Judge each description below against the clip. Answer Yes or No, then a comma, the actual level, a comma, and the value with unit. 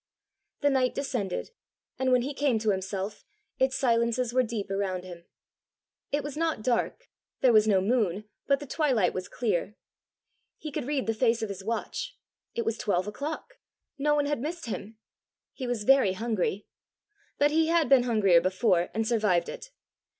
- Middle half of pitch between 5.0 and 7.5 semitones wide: Yes, average, 5.3 semitones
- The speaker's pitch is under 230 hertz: No, high, 235 Hz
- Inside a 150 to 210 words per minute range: Yes, average, 170 wpm